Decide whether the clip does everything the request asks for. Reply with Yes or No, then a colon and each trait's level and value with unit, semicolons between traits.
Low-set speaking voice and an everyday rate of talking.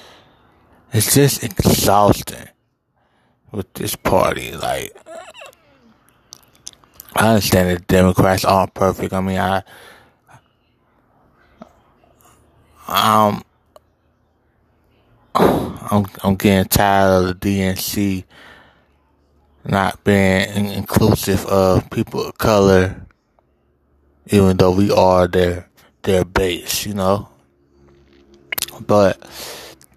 No: very low, 95 Hz; slow, 90 wpm